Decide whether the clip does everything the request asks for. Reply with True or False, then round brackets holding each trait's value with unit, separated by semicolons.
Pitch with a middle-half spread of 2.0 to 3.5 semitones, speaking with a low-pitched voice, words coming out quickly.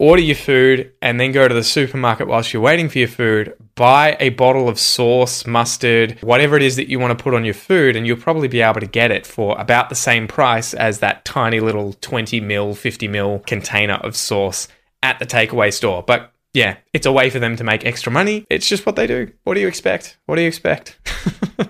True (3.1 semitones; 120 Hz; 230 wpm)